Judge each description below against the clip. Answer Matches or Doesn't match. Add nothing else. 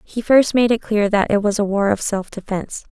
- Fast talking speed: Matches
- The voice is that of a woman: Matches